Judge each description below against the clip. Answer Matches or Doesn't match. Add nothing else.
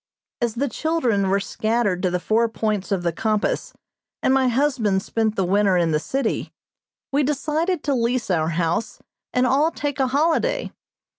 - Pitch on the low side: Doesn't match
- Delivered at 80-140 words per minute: Doesn't match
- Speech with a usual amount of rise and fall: Doesn't match